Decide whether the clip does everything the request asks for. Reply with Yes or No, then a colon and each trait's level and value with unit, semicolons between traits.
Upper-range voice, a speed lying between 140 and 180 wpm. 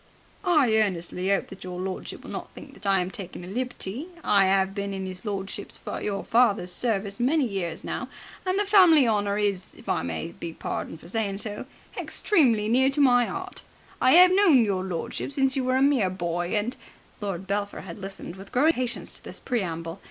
No: high, 205 Hz; average, 200 wpm